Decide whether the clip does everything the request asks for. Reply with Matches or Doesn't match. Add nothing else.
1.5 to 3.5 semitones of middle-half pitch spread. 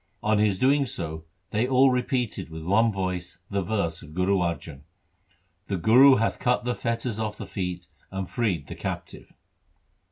Doesn't match